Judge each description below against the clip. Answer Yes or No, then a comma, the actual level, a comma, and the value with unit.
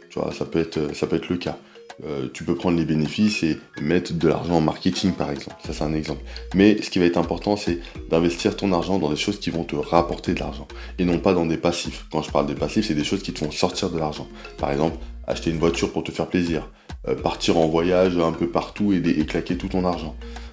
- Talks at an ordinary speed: No, fast, 255 wpm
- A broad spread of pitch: No, average, 2.7 semitones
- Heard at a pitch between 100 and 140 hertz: No, very low, 85 Hz